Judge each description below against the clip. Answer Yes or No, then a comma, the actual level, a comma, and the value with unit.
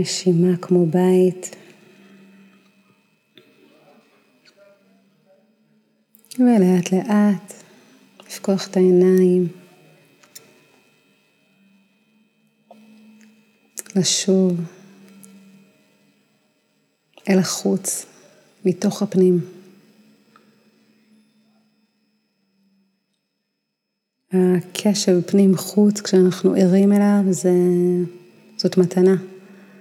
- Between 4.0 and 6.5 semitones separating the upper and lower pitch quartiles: No, narrow, 2.5 semitones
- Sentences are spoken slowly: Yes, slow, 40 wpm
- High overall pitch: Yes, high, 195 Hz